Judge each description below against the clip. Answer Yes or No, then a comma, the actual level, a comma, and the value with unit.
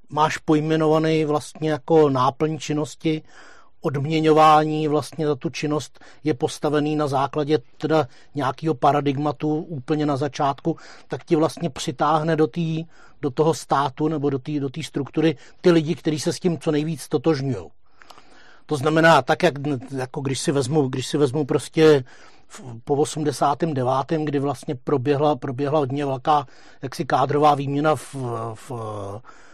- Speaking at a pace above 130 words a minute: Yes, average, 140 wpm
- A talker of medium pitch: Yes, medium, 150 Hz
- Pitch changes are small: Yes, narrow, 1.8 semitones